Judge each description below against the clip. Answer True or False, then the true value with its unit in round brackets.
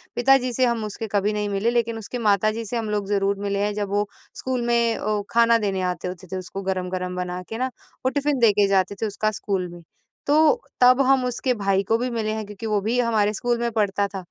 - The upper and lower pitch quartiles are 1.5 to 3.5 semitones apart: True (3.0 semitones)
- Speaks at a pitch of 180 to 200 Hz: False (215 Hz)